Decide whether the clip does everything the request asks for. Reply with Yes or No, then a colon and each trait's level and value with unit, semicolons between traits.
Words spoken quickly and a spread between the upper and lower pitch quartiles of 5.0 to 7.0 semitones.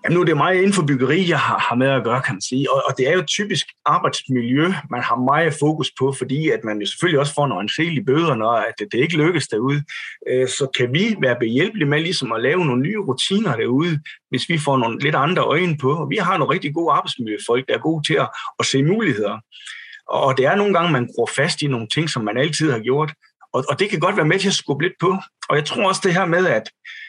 Yes: fast, 250 wpm; wide, 5.4 semitones